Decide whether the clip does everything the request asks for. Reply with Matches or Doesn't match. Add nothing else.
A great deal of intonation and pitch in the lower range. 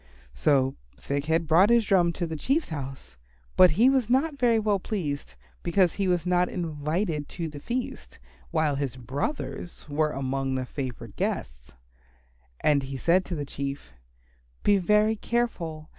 Doesn't match